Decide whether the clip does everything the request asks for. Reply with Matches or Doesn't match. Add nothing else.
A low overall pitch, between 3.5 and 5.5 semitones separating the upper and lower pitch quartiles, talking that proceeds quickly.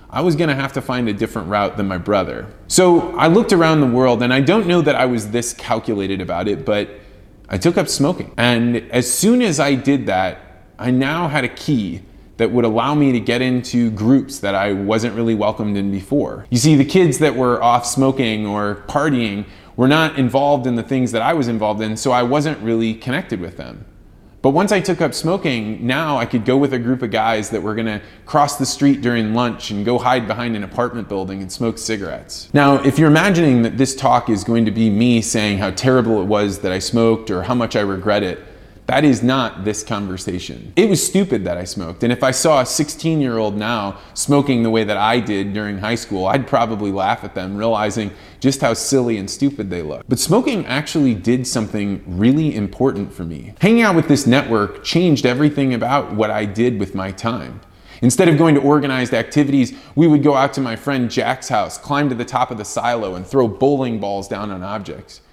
Matches